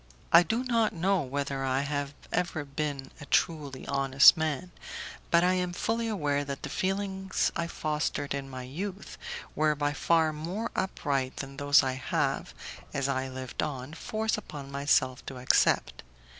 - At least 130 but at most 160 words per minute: Yes, average, 155 wpm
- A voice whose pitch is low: No, medium, 145 Hz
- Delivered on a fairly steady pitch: No, average, 4.5 semitones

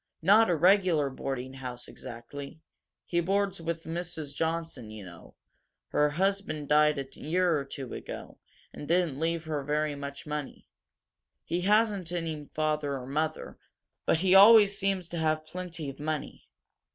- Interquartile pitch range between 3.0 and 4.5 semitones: Yes, average, 3.8 semitones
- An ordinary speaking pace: Yes, average, 150 wpm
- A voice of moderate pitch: Yes, medium, 155 Hz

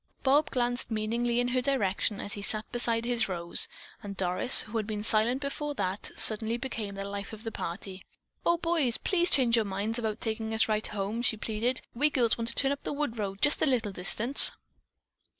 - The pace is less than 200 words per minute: No, fast, 205 wpm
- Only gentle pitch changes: No, average, 3.3 semitones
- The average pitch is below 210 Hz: No, high, 225 Hz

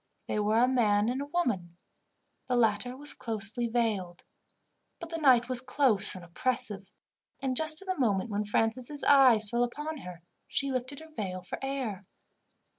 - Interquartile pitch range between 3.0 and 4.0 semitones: No, average, 4.7 semitones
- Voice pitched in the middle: No, high, 240 Hz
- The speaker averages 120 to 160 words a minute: No, average, 170 wpm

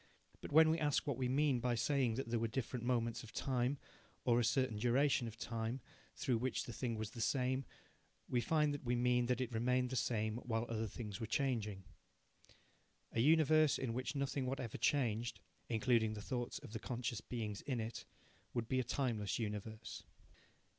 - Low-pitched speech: Yes, low, 120 Hz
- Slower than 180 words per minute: No, average, 190 wpm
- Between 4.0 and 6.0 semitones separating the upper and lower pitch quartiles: No, narrow, 2.6 semitones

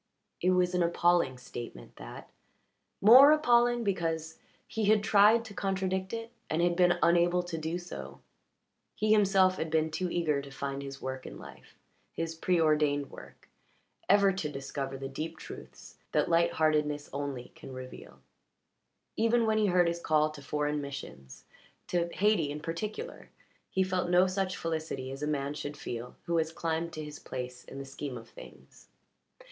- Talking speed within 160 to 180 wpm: Yes, average, 170 wpm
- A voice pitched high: No, medium, 165 Hz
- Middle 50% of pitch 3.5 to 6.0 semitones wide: Yes, average, 4.5 semitones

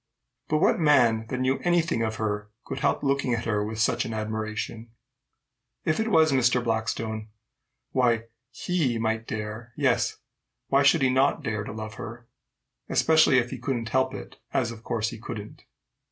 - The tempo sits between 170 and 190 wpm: Yes, average, 175 wpm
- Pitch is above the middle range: No, low, 115 Hz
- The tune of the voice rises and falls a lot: No, average, 3.5 semitones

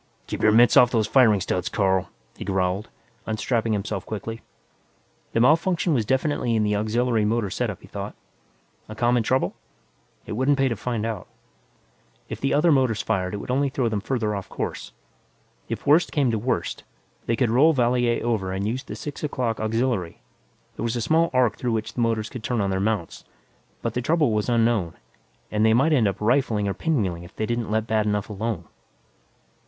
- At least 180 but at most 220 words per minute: Yes, average, 195 wpm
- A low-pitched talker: Yes, low, 115 Hz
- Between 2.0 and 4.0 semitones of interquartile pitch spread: Yes, average, 3.2 semitones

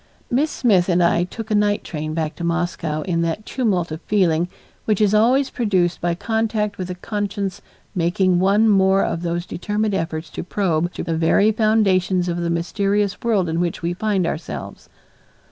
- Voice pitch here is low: No, medium, 185 Hz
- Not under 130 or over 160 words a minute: No, average, 180 wpm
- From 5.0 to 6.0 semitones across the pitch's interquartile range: No, average, 3.5 semitones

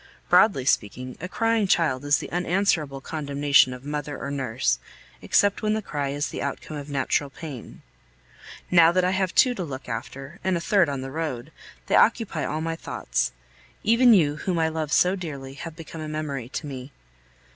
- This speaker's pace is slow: No, average, 190 wpm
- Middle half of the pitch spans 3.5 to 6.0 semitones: Yes, average, 4.6 semitones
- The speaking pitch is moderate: Yes, medium, 150 Hz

